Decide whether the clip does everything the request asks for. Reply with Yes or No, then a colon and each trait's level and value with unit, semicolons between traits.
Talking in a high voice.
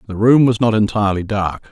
No: low, 105 Hz